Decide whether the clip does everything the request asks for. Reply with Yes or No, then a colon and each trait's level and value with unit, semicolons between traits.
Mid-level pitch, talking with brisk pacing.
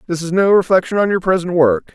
Yes: medium, 175 Hz; fast, 245 wpm